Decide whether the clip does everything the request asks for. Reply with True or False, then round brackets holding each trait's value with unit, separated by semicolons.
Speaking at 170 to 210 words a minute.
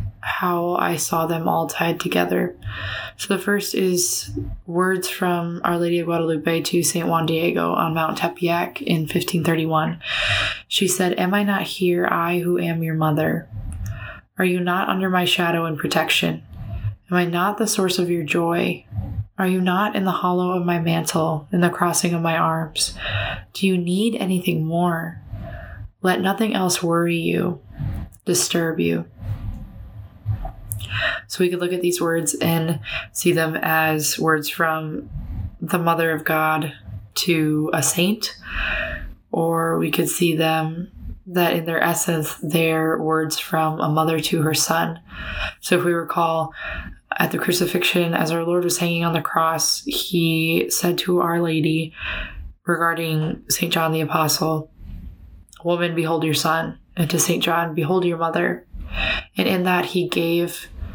False (155 wpm)